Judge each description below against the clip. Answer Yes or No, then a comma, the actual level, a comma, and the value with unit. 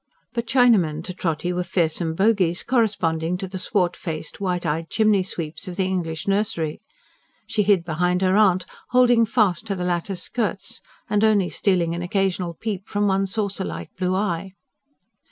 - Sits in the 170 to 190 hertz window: Yes, medium, 185 Hz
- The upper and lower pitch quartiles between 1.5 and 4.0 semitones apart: Yes, average, 3.2 semitones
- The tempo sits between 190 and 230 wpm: No, average, 170 wpm